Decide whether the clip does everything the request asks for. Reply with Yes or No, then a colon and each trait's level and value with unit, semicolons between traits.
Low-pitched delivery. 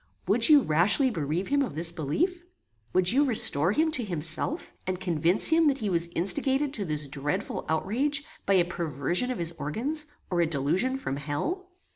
No: medium, 185 Hz